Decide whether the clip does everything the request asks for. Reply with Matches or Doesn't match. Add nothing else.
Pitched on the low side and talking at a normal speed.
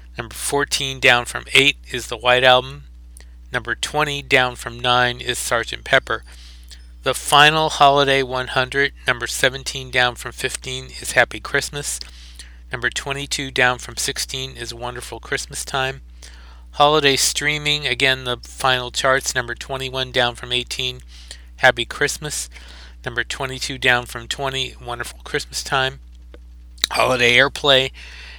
Doesn't match